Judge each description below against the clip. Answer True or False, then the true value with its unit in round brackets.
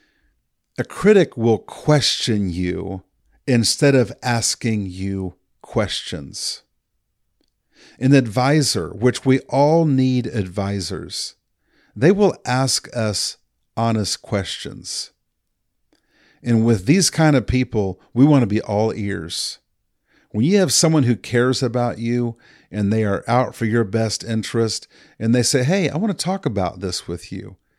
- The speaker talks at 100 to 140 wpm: True (135 wpm)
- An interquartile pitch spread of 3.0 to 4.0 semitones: False (4.4 semitones)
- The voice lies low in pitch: True (115 Hz)